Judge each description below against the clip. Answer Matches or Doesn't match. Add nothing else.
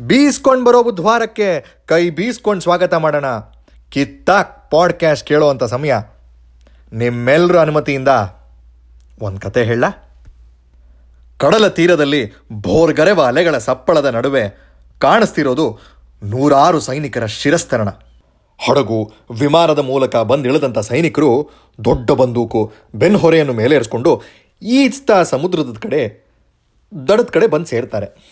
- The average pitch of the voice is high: Doesn't match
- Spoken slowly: Doesn't match